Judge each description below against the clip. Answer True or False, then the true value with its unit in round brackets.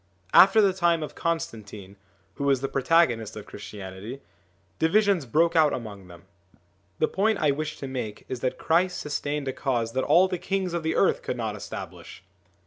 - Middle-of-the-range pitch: True (145 Hz)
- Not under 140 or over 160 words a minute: False (180 wpm)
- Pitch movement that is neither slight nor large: False (6.7 semitones)